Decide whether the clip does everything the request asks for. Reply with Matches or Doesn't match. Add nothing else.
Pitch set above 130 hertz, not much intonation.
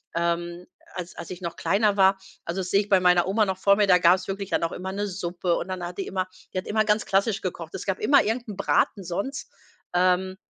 Matches